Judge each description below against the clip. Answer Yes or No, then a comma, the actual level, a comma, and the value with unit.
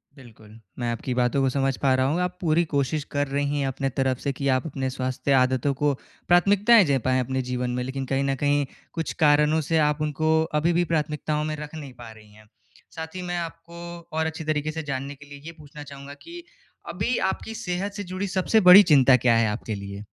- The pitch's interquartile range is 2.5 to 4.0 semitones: Yes, average, 3.6 semitones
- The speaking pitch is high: No, medium, 145 Hz